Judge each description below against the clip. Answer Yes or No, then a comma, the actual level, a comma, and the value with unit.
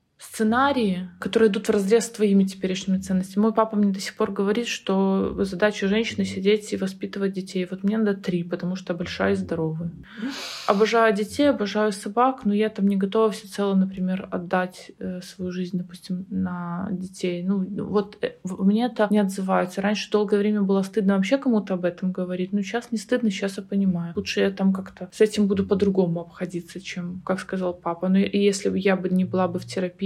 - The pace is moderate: No, fast, 200 wpm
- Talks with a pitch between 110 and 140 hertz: No, high, 195 Hz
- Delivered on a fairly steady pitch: Yes, narrow, 2.3 semitones